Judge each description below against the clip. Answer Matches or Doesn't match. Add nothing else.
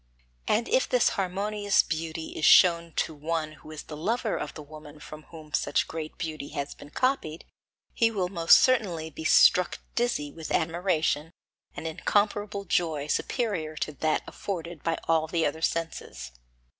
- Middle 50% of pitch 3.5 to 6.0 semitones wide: Matches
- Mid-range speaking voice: Matches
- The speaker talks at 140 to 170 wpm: Matches